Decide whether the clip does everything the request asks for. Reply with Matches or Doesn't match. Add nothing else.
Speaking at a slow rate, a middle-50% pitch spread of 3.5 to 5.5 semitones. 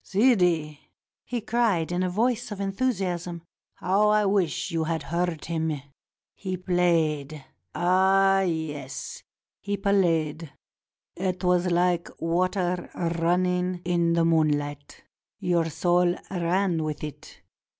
Doesn't match